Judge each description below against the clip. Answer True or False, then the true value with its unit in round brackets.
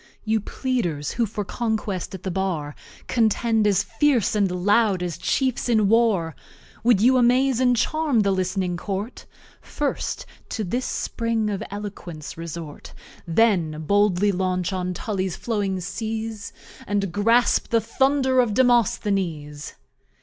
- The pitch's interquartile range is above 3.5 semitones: True (4.2 semitones)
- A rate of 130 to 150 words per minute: True (135 wpm)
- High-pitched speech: True (205 Hz)